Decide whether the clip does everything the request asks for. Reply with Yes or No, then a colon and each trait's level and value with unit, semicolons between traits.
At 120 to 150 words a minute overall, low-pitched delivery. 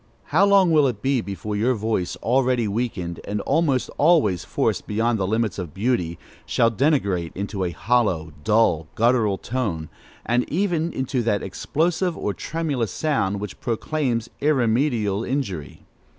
Yes: average, 145 wpm; low, 115 Hz